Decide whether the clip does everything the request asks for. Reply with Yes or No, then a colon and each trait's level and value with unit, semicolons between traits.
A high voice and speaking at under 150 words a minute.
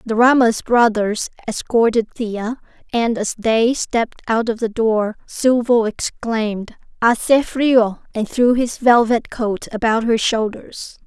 Yes: high, 230 Hz; slow, 135 wpm